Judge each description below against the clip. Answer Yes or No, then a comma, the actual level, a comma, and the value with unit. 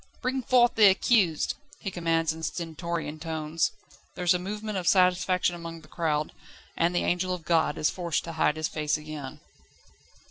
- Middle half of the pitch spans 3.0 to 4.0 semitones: No, narrow, 2.5 semitones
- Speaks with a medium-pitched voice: Yes, medium, 170 Hz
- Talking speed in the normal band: Yes, average, 175 wpm